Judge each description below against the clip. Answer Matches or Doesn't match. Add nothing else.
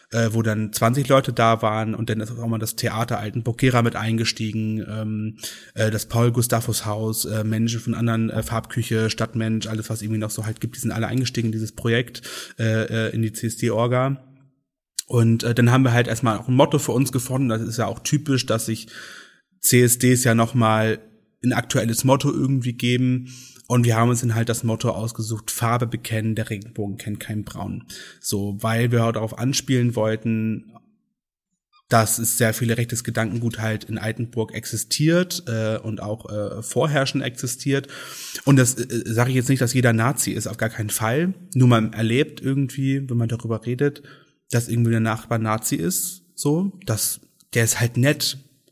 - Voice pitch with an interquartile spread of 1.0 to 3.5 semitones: Matches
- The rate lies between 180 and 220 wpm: Matches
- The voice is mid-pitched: Doesn't match